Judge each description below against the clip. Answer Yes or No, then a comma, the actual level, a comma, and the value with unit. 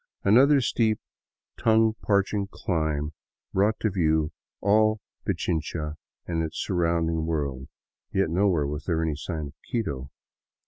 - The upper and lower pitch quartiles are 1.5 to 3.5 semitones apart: No, average, 4.8 semitones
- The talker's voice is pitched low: Yes, very low, 85 Hz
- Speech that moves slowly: Yes, slow, 125 wpm